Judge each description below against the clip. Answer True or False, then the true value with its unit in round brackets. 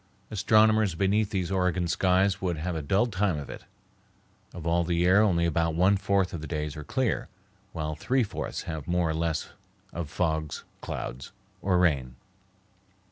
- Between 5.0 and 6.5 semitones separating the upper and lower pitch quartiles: False (3.5 semitones)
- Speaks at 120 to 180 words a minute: True (170 wpm)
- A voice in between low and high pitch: False (90 Hz)